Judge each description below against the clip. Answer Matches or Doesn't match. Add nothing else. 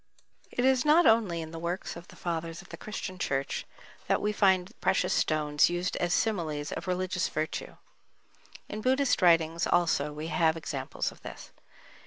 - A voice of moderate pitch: Matches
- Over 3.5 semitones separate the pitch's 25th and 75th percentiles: Matches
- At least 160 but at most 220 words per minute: Matches